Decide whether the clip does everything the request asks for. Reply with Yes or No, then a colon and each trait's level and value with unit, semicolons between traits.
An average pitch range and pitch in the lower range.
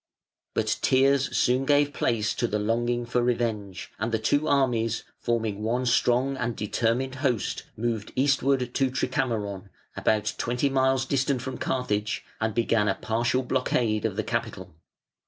Yes: average, 3.0 semitones; low, 120 Hz